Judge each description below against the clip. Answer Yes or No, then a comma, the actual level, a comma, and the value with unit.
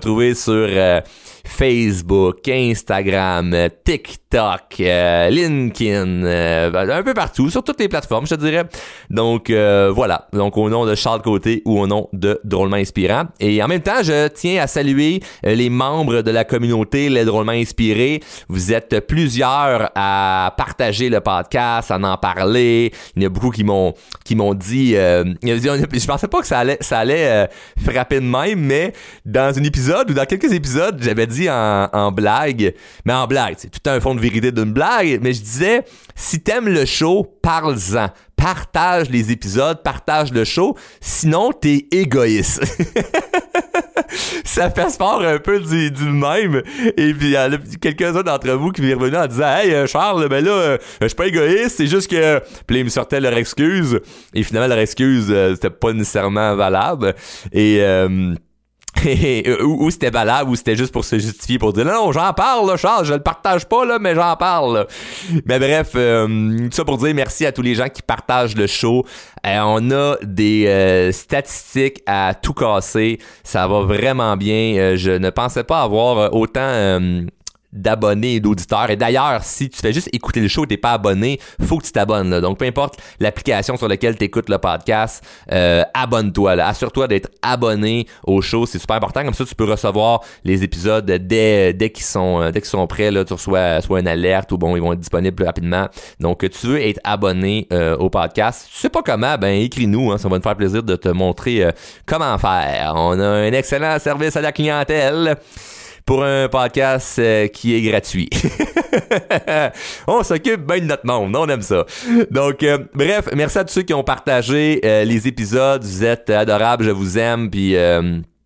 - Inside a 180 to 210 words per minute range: Yes, average, 190 wpm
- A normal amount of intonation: No, wide, 5.7 semitones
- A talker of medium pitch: No, low, 115 Hz